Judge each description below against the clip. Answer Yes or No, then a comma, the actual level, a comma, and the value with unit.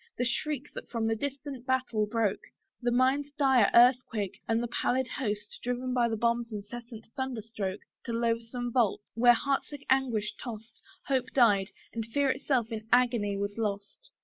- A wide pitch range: No, average, 2.8 semitones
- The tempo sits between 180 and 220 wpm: No, average, 170 wpm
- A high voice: Yes, high, 235 Hz